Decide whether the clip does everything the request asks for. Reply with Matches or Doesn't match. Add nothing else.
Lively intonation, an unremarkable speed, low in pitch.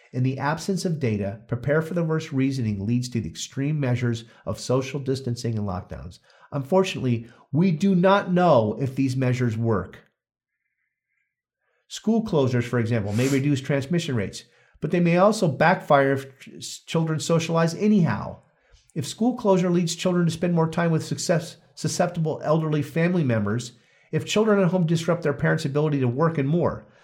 Doesn't match